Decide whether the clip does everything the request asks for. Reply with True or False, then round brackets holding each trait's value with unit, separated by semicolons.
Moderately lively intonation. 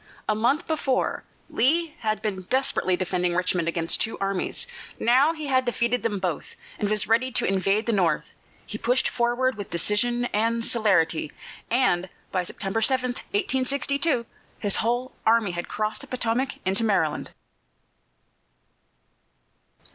True (4.9 semitones)